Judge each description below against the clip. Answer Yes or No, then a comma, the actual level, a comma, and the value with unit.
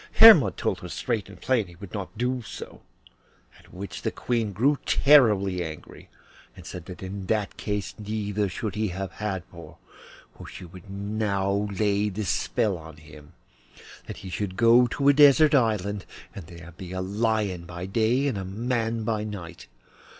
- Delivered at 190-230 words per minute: No, average, 175 wpm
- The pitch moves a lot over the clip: No, average, 3.4 semitones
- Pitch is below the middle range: Yes, low, 100 Hz